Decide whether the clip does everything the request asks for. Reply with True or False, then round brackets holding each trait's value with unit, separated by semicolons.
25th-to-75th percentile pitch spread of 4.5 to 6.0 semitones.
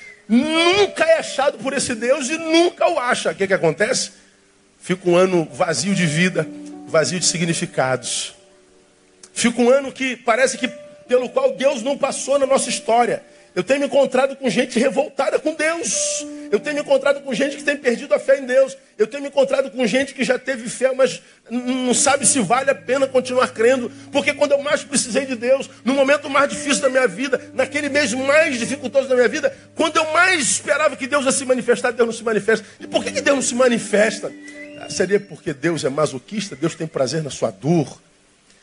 True (5.1 semitones)